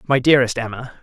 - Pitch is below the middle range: Yes, low, 125 Hz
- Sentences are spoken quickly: No, average, 175 wpm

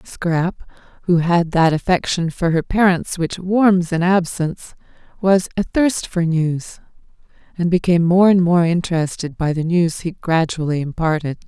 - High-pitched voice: No, medium, 170 Hz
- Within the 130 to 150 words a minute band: Yes, average, 145 wpm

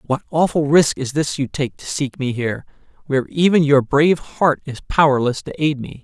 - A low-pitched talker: No, medium, 145 Hz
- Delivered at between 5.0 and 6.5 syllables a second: Yes, 5.3 syllables/s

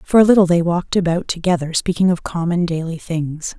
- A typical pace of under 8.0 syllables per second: Yes, 5.8 syllables/s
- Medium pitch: Yes, medium, 170 Hz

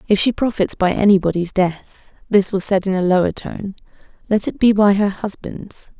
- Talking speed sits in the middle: Yes, average, 190 wpm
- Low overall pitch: No, high, 195 Hz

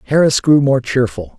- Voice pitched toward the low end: Yes, low, 125 Hz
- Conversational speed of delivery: Yes, average, 175 wpm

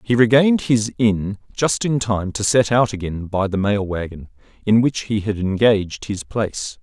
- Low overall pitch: Yes, low, 105 Hz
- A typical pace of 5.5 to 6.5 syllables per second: No, 4.7 syllables/s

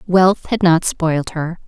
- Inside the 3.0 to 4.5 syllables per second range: Yes, 4.0 syllables/s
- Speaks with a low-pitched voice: No, medium, 170 Hz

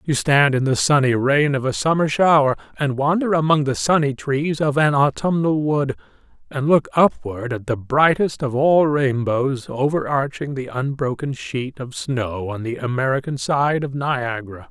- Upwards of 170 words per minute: No, average, 165 wpm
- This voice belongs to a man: Yes, male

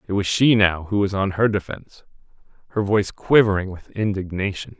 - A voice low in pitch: Yes, low, 100 Hz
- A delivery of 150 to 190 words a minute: Yes, average, 175 wpm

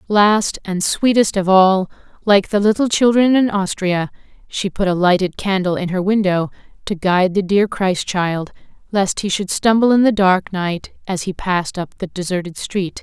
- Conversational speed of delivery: Yes, average, 185 wpm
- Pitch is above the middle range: Yes, high, 195 Hz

